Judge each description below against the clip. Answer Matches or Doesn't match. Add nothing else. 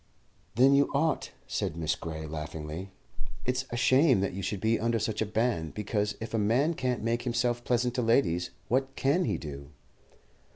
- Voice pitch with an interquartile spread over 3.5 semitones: Matches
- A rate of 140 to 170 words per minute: Doesn't match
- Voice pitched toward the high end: Doesn't match